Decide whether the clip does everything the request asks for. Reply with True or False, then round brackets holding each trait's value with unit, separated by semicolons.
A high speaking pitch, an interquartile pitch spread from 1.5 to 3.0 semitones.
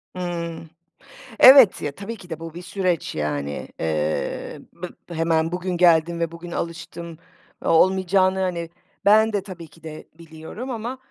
False (170 Hz; 2.5 semitones)